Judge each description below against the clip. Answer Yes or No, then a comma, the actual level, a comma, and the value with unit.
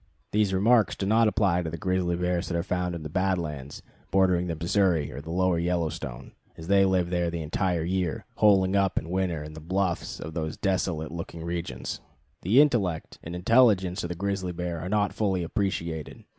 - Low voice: Yes, very low, 90 Hz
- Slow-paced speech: No, average, 195 wpm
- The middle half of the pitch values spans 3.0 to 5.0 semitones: No, narrow, 2.4 semitones